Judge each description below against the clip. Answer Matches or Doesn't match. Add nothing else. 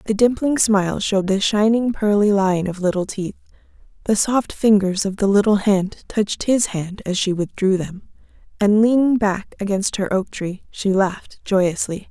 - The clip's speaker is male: Doesn't match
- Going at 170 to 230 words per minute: Matches